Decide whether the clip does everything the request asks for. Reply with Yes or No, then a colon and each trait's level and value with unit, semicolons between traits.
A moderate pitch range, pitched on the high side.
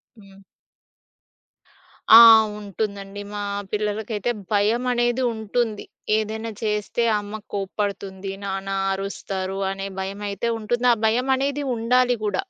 Yes: average, 3.0 semitones; high, 210 Hz